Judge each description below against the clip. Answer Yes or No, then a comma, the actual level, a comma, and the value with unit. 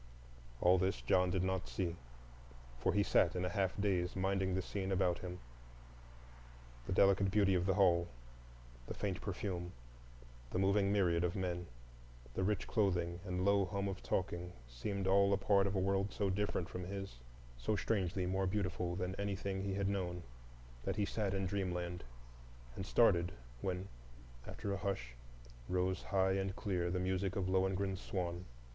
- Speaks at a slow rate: No, average, 165 wpm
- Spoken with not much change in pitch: Yes, narrow, 1.6 semitones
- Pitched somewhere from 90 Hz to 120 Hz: Yes, very low, 95 Hz